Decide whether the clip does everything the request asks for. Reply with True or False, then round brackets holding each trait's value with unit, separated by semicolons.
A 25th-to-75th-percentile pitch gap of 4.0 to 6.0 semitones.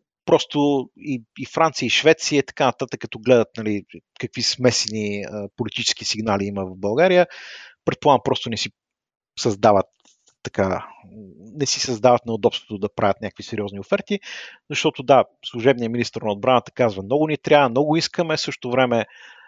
True (4.6 semitones)